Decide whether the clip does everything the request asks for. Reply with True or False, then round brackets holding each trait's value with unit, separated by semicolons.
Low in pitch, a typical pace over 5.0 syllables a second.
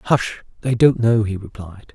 False (110 Hz; 4.1 syllables/s)